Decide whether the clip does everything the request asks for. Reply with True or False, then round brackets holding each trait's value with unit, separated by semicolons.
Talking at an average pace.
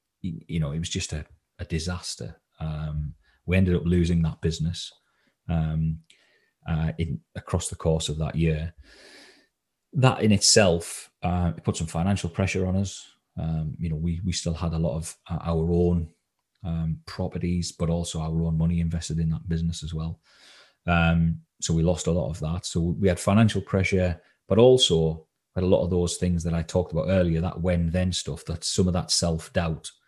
True (190 wpm)